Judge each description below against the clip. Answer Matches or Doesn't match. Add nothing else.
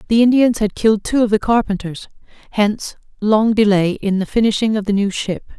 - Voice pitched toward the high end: Matches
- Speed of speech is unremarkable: Matches